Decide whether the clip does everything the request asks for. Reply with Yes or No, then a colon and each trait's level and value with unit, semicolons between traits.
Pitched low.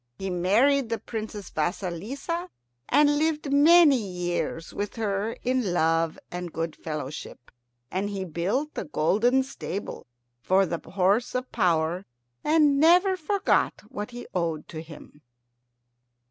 No: high, 205 Hz